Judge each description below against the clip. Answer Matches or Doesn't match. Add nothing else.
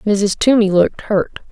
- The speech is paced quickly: Doesn't match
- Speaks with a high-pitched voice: Matches